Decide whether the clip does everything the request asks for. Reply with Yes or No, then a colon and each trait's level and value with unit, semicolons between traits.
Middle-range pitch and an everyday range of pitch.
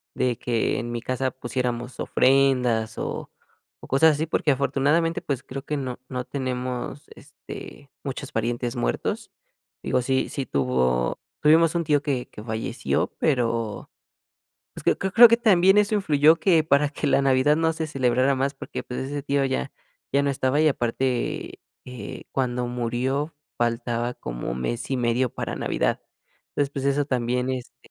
No: low, 130 Hz; average, 3.1 semitones